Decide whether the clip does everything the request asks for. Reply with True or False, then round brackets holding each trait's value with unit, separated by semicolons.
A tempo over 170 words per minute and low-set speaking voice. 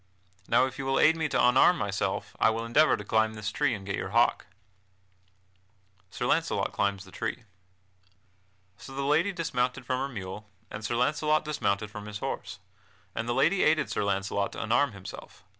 True (190 wpm; 115 Hz)